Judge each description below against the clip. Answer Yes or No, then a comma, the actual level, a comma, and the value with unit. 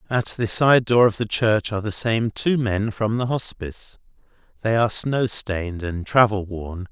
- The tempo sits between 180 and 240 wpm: Yes, average, 190 wpm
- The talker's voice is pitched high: No, low, 110 Hz